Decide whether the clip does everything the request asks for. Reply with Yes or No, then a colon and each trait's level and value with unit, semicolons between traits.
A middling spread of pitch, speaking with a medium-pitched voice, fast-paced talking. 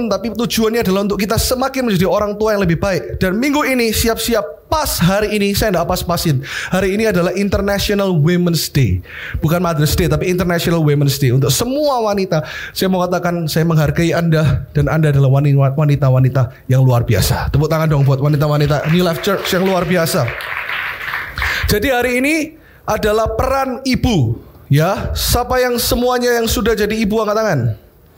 No: wide, 6.7 semitones; medium, 180 Hz; fast, 165 wpm